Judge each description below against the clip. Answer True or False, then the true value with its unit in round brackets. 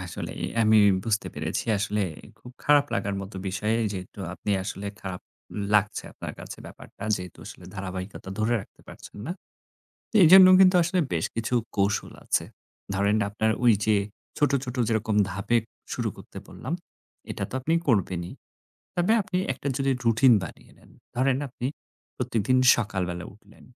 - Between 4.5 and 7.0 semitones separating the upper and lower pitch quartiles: True (4.8 semitones)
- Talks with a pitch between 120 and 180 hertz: False (110 Hz)